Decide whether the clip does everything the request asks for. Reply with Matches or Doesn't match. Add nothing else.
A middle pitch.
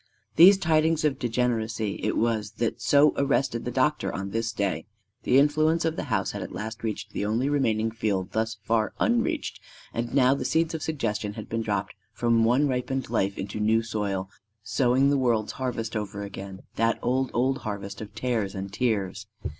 Doesn't match